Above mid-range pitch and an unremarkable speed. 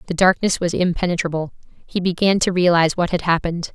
No: medium, 175 Hz; average, 175 wpm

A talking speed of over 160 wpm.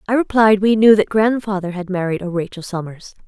Yes: average, 200 wpm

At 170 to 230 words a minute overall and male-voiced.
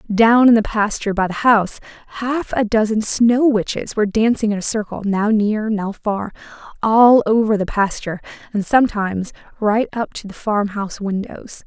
No: average, 175 wpm; female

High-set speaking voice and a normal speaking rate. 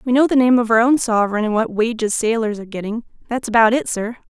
No: high, 230 Hz; fast, 250 wpm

